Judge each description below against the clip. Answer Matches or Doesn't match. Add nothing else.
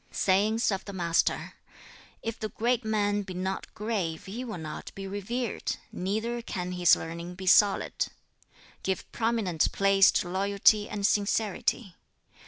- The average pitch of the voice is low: Doesn't match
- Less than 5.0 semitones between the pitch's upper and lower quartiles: Matches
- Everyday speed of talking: Matches